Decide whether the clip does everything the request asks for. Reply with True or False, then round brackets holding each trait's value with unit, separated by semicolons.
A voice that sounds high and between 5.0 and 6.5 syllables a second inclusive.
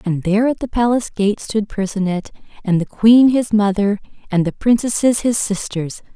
True (210 Hz; 5.1 syllables/s)